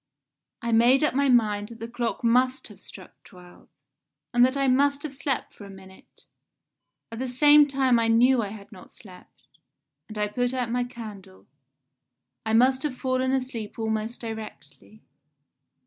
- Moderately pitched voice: No, high, 235 Hz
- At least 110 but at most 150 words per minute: No, average, 165 wpm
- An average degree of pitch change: Yes, average, 3.3 semitones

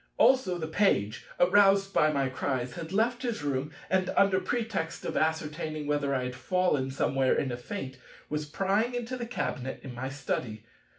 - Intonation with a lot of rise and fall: Yes, wide, 6.7 semitones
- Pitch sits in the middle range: Yes, medium, 155 Hz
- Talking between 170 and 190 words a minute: Yes, average, 175 wpm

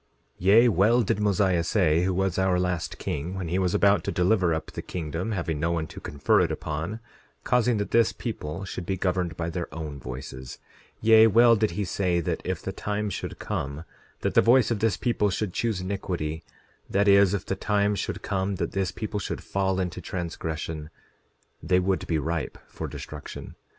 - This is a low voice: Yes, very low, 95 Hz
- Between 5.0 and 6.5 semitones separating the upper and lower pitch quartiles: No, average, 3.6 semitones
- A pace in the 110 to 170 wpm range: No, average, 195 wpm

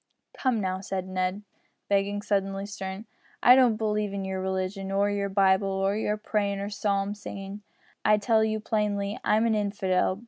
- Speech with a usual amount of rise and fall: No, narrow, 1.5 semitones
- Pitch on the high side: Yes, high, 200 Hz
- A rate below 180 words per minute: Yes, average, 170 wpm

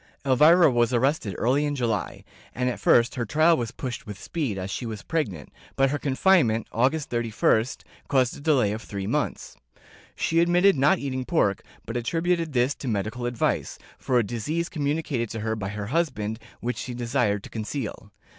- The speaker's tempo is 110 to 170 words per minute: No, average, 180 wpm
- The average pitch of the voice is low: Yes, low, 125 Hz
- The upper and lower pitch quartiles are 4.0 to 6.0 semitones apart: Yes, average, 5.0 semitones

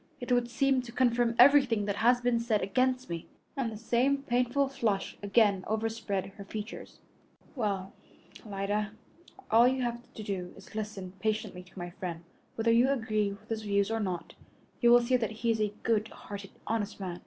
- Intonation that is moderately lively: Yes, average, 3.2 semitones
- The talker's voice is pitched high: Yes, high, 220 Hz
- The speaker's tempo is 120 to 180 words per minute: No, average, 190 wpm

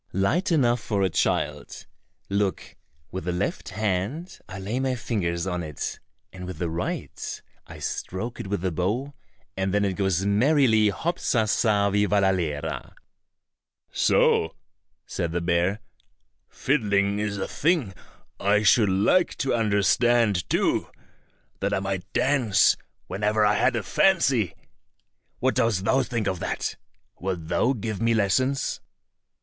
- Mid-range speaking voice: No, low, 100 Hz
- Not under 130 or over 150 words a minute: Yes, average, 140 wpm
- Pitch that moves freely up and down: No, average, 4.0 semitones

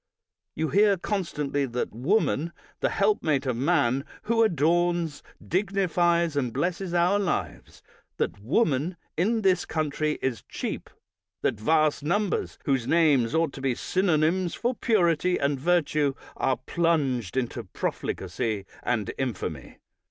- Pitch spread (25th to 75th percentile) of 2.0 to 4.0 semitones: No, average, 5.0 semitones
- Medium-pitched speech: Yes, medium, 155 Hz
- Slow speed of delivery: Yes, slow, 125 wpm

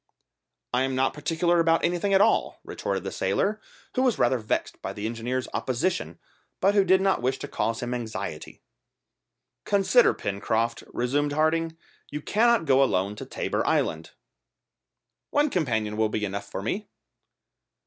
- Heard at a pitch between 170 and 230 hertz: No, low, 135 Hz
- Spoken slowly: No, average, 155 wpm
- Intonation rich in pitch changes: Yes, wide, 7.9 semitones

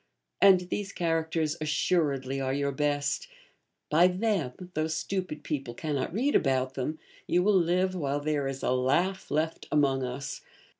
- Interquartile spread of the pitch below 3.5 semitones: No, average, 4.6 semitones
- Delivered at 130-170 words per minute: Yes, average, 150 wpm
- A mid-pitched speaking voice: Yes, medium, 155 Hz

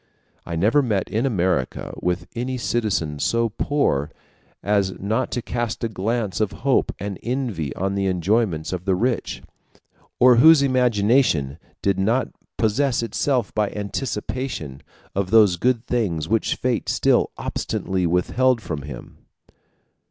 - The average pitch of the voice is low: Yes, low, 105 Hz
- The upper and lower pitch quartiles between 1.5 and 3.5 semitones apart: No, average, 4.9 semitones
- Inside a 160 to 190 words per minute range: No, slow, 135 wpm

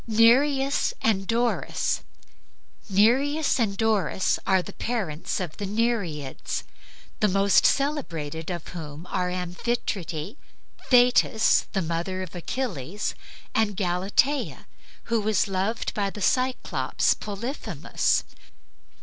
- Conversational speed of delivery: No, slow, 105 wpm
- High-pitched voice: Yes, high, 200 Hz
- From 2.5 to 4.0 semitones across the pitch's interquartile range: No, average, 4.7 semitones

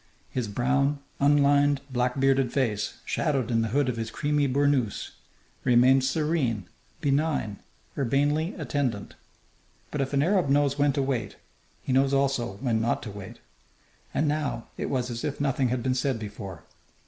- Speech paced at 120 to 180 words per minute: Yes, average, 160 wpm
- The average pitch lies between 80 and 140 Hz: Yes, low, 135 Hz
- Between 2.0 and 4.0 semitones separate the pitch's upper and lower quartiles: Yes, average, 3.3 semitones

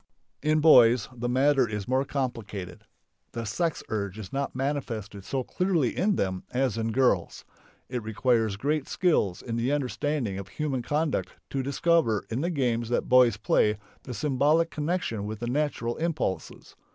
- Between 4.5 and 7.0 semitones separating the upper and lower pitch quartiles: Yes, average, 4.9 semitones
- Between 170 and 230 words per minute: No, average, 160 wpm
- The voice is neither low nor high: No, low, 125 Hz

